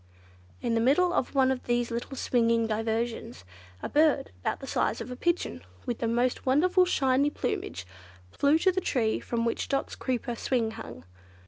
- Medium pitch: No, very high, 250 Hz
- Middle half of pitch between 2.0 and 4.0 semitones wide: Yes, average, 3.4 semitones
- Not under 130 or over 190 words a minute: Yes, average, 180 wpm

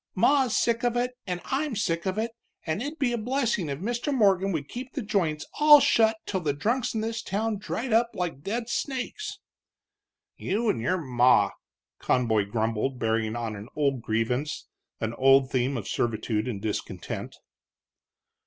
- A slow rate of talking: No, average, 170 wpm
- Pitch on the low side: No, medium, 180 Hz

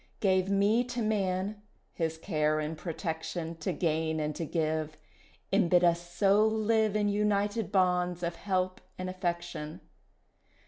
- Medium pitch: Yes, medium, 180 Hz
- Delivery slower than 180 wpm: Yes, average, 140 wpm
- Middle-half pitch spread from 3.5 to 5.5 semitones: Yes, average, 3.9 semitones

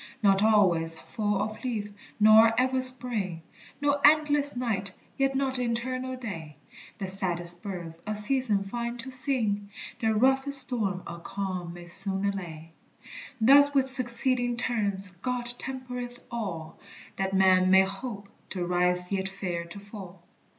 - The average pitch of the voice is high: Yes, high, 210 Hz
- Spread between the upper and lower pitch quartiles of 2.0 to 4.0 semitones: No, average, 5.1 semitones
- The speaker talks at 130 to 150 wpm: Yes, average, 140 wpm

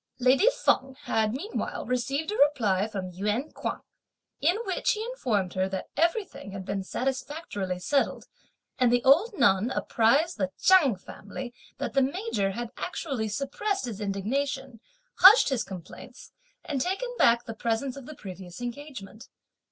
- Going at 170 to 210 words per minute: No, average, 150 wpm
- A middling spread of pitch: No, wide, 6.4 semitones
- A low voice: No, very high, 250 Hz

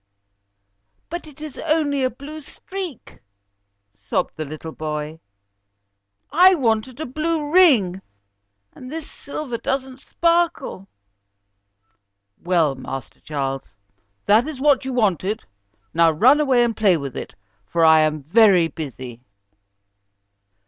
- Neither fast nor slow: No, slow, 120 wpm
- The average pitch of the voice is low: No, high, 235 Hz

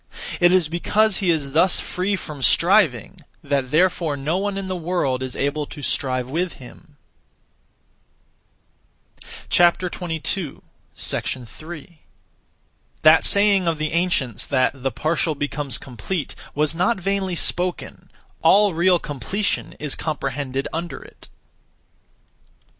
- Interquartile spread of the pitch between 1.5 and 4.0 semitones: No, average, 4.5 semitones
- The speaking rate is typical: No, slow, 115 wpm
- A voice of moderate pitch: Yes, medium, 160 Hz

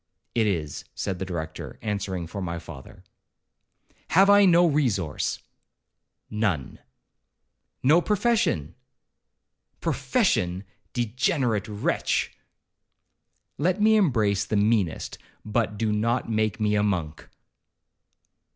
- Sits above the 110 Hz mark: No, low, 105 Hz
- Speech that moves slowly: Yes, slow, 100 wpm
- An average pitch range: No, wide, 5.8 semitones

